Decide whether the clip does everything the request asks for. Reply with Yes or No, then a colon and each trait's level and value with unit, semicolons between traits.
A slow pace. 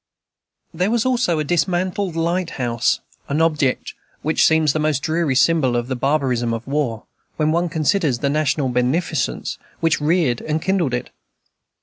No: average, 155 wpm